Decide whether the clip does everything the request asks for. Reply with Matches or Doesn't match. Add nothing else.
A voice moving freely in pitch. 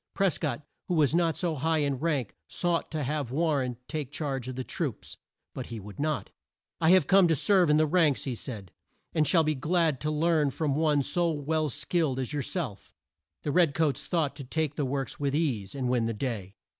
Doesn't match